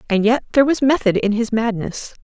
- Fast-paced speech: Yes, fast, 215 wpm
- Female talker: Yes, female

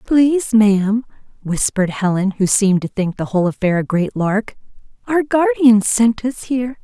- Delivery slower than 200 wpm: Yes, average, 165 wpm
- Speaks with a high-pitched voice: Yes, high, 220 Hz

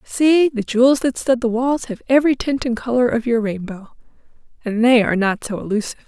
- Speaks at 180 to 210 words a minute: Yes, average, 200 wpm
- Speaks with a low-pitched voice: No, high, 240 Hz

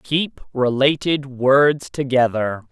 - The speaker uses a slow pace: Yes, slow, 90 wpm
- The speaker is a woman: No, male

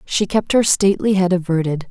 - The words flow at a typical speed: Yes, average, 190 wpm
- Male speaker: No, female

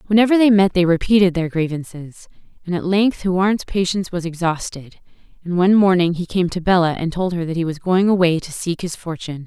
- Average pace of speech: No, fast, 210 wpm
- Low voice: No, medium, 180 Hz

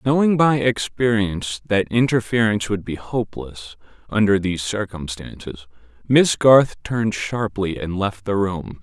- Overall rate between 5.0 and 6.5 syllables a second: No, 4.5 syllables/s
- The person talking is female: No, male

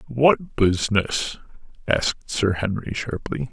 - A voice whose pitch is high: No, low, 110 Hz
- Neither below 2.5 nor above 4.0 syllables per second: Yes, 3.9 syllables/s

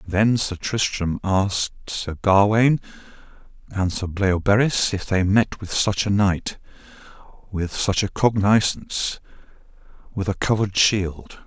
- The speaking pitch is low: Yes, low, 100 Hz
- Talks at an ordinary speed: No, slow, 125 wpm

